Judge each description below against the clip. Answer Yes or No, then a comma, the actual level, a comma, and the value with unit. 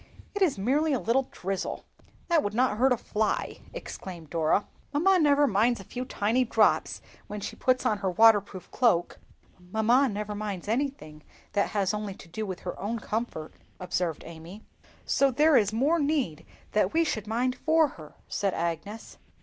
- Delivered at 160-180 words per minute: Yes, average, 175 wpm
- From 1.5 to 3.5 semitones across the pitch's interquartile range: No, average, 5.3 semitones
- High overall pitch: Yes, high, 215 Hz